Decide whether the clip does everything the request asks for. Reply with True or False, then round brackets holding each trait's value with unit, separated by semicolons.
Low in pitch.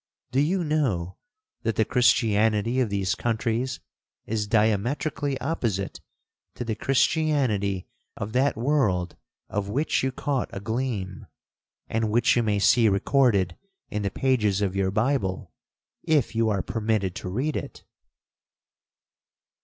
True (110 Hz)